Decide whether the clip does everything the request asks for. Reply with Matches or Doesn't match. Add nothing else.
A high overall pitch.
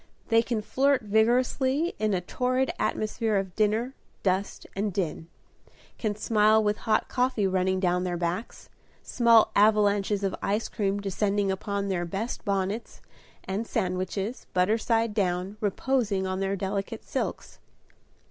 Matches